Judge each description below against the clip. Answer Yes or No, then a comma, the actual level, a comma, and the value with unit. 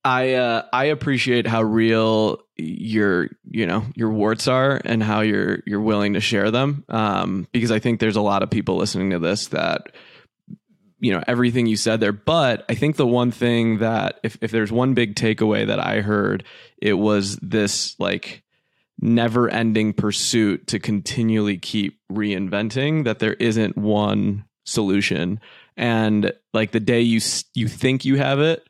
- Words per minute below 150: No, average, 170 wpm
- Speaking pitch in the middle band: No, low, 110 Hz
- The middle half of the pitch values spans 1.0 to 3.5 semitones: Yes, narrow, 2.5 semitones